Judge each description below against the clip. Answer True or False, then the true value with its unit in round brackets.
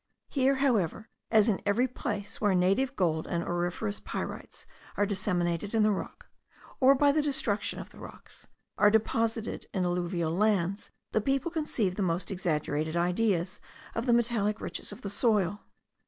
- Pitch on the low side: False (205 Hz)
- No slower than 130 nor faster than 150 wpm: False (160 wpm)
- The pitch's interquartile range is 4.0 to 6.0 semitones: True (4.3 semitones)